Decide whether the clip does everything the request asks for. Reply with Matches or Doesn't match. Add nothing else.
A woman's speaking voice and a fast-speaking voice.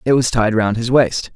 Doesn't match